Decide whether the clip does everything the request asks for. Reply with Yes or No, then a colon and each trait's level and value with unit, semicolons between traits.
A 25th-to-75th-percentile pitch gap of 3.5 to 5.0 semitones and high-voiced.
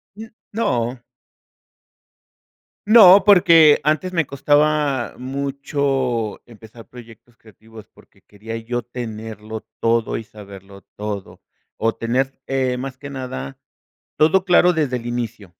No: average, 4.4 semitones; low, 125 Hz